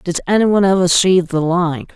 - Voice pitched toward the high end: No, medium, 180 Hz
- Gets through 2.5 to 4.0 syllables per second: No, 4.9 syllables/s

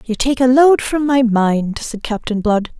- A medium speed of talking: No, fast, 215 wpm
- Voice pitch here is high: Yes, high, 240 Hz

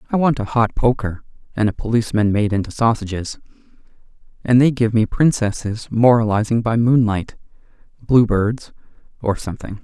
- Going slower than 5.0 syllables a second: No, 5.3 syllables/s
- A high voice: No, low, 110 Hz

